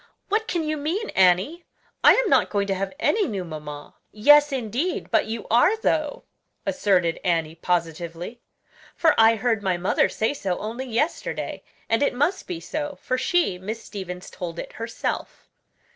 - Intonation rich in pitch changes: Yes, wide, 8.4 semitones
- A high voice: Yes, high, 225 Hz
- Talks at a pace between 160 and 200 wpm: Yes, average, 165 wpm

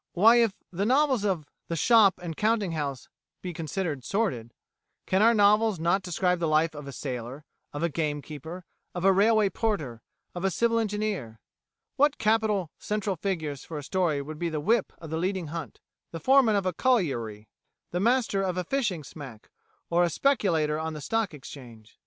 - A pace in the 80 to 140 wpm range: No, average, 180 wpm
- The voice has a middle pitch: Yes, medium, 180 Hz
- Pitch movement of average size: No, wide, 5.8 semitones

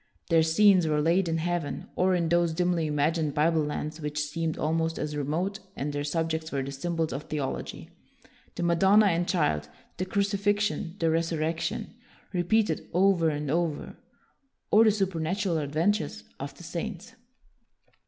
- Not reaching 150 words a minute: No, average, 155 wpm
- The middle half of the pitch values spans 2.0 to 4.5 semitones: Yes, average, 3.1 semitones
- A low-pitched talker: No, medium, 165 Hz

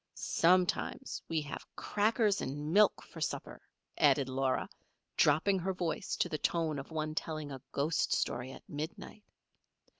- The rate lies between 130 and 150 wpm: Yes, average, 145 wpm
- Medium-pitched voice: Yes, medium, 155 Hz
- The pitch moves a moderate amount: Yes, average, 4.2 semitones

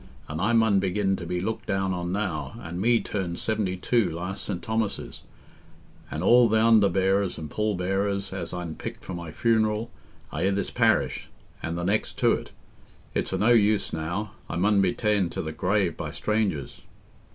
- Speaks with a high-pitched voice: No, very low, 95 Hz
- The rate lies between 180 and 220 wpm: Yes, average, 185 wpm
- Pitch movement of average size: Yes, average, 3.4 semitones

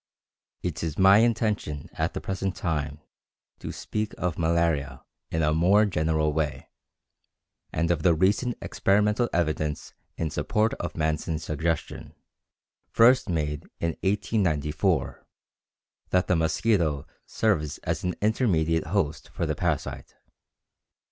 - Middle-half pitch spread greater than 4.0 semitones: Yes, average, 4.5 semitones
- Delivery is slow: Yes, slow, 120 wpm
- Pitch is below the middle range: Yes, very low, 85 Hz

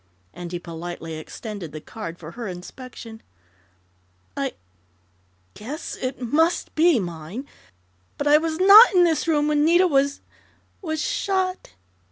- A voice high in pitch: Yes, very high, 275 Hz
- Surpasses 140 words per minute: No, slow, 135 wpm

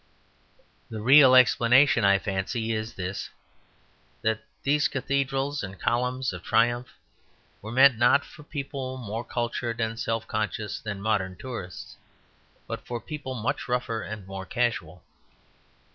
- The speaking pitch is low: Yes, low, 115 Hz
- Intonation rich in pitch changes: No, average, 3.6 semitones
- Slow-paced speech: Yes, slow, 130 wpm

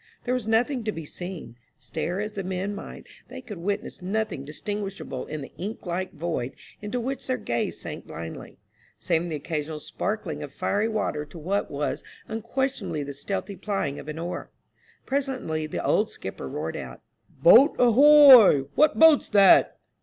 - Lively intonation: Yes, wide, 6.6 semitones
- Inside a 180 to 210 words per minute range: No, average, 165 wpm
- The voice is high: Yes, high, 195 Hz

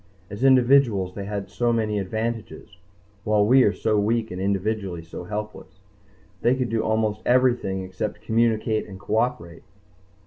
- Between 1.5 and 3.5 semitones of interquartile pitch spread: Yes, average, 2.8 semitones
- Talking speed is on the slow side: No, average, 145 wpm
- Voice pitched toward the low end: Yes, low, 110 Hz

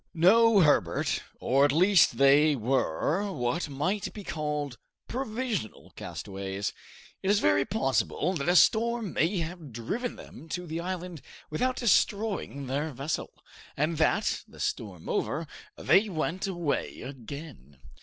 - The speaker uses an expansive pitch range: Yes, wide, 6.1 semitones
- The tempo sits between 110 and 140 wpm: Yes, slow, 135 wpm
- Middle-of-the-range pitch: Yes, medium, 160 Hz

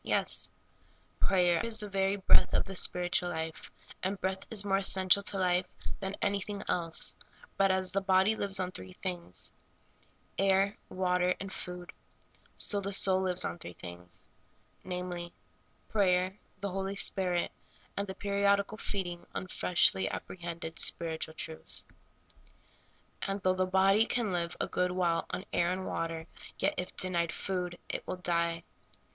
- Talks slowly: No, average, 155 wpm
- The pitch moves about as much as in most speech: No, narrow, 2.0 semitones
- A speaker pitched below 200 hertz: Yes, medium, 185 Hz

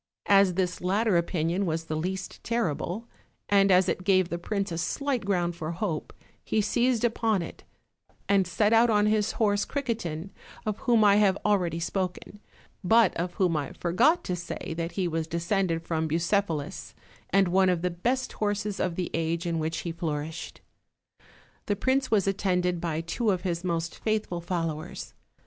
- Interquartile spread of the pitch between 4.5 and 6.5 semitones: No, average, 3.6 semitones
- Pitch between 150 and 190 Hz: Yes, medium, 185 Hz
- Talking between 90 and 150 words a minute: No, average, 175 wpm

